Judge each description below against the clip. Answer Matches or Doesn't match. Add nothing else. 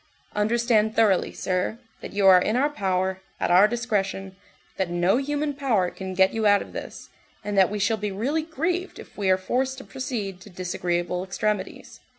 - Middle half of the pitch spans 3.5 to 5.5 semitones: Matches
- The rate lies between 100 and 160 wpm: Doesn't match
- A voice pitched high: Matches